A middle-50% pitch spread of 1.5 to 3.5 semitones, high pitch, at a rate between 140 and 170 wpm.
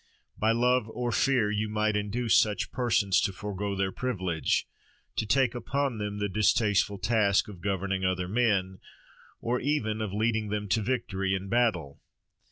No: average, 3.2 semitones; low, 105 Hz; average, 160 wpm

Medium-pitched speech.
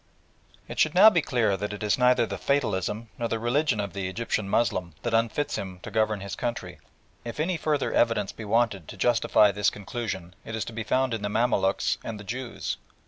No: low, 110 Hz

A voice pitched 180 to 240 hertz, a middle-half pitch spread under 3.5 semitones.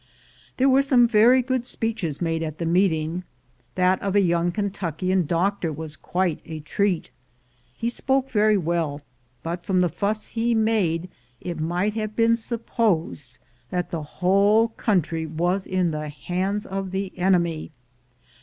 No: medium, 185 Hz; average, 4.3 semitones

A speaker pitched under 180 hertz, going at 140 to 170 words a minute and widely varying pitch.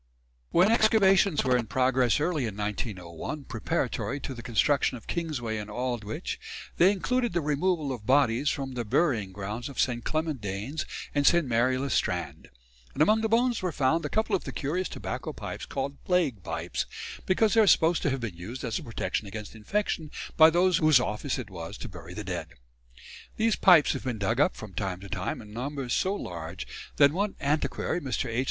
No: low, 135 Hz; average, 195 wpm; wide, 7.3 semitones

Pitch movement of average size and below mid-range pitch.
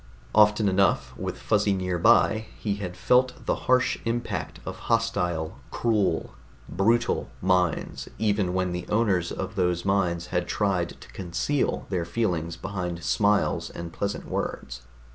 Yes: average, 3.4 semitones; very low, 95 Hz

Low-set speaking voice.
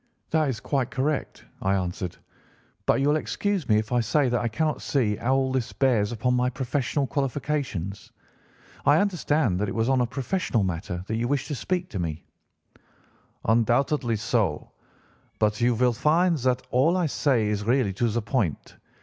Yes: low, 125 Hz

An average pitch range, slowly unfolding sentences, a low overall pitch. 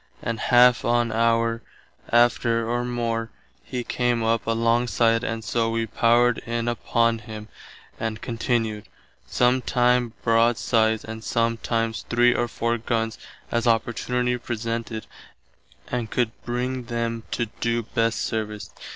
No: narrow, 1.1 semitones; slow, 125 wpm; low, 115 Hz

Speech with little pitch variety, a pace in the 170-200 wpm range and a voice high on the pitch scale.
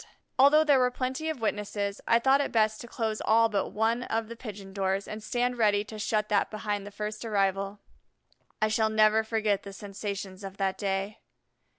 Yes: narrow, 2.2 semitones; average, 195 wpm; high, 215 Hz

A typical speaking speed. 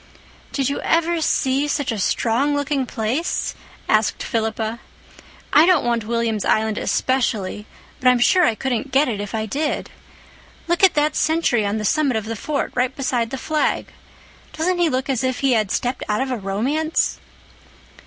Yes: average, 175 wpm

